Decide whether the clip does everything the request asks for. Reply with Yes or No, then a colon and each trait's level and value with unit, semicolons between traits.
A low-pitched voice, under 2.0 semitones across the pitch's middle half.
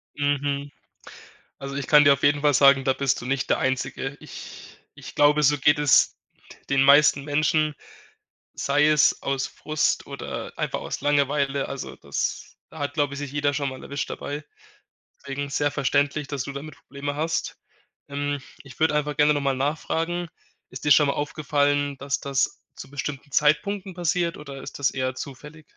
No: medium, 145 Hz; narrow, 1.2 semitones